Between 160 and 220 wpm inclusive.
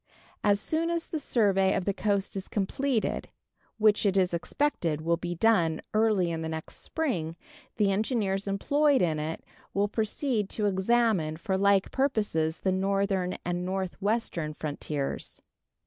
No: average, 145 wpm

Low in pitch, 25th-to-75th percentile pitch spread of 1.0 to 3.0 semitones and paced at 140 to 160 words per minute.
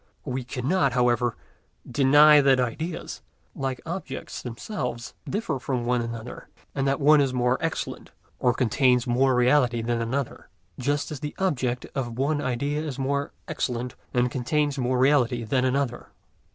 Yes: low, 130 Hz; average, 2.7 semitones; average, 150 wpm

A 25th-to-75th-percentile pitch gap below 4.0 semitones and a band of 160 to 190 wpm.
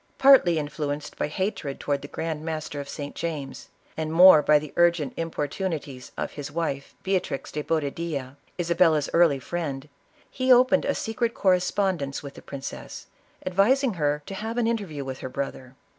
No: average, 4.6 semitones; average, 170 wpm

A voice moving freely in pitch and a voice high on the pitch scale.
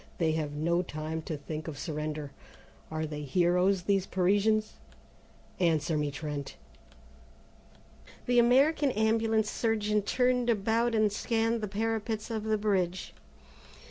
Yes: wide, 5.9 semitones; high, 195 Hz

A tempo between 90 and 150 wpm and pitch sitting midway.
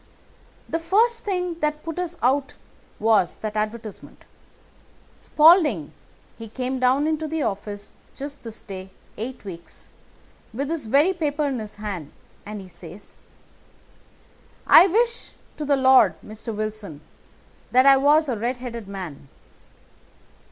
No: slow, 135 wpm; very high, 255 Hz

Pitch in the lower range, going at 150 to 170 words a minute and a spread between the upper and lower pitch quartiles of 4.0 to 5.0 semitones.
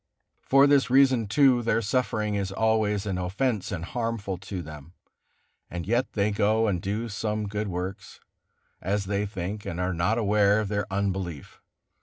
No: low, 105 Hz; average, 165 wpm; average, 2.8 semitones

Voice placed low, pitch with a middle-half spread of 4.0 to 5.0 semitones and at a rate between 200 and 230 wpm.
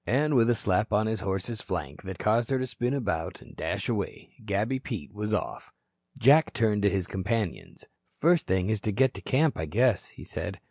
Yes: low, 110 Hz; average, 4.5 semitones; fast, 205 wpm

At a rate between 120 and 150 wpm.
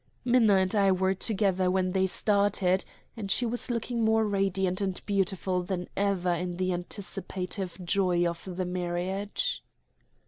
Yes: average, 145 wpm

